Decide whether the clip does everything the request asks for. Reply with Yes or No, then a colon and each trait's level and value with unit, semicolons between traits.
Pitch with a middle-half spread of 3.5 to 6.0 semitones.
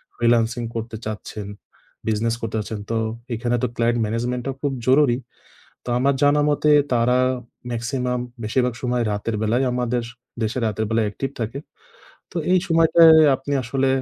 No: average, 2.7 semitones